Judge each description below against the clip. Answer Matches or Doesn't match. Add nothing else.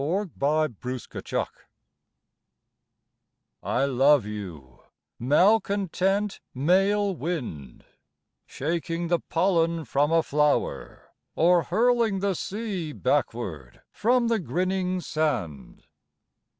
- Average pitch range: Doesn't match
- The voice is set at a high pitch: Doesn't match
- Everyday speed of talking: Doesn't match